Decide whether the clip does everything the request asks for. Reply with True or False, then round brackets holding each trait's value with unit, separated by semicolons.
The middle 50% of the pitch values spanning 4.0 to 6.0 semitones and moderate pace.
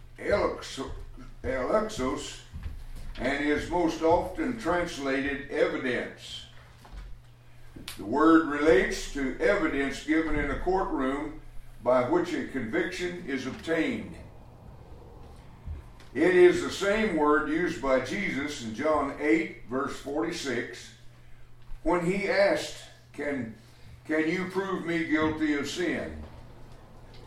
False (5.2 semitones; 100 wpm)